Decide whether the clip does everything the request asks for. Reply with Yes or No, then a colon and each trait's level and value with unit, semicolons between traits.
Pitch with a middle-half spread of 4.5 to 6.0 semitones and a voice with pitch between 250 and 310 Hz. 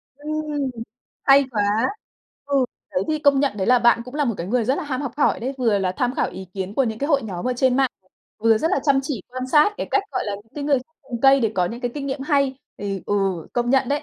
No: average, 3.9 semitones; very high, 260 Hz